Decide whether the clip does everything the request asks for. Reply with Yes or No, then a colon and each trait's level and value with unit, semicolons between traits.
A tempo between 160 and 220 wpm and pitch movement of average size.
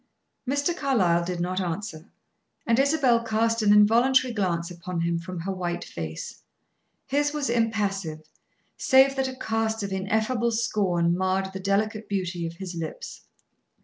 No: average, 150 wpm; average, 4.9 semitones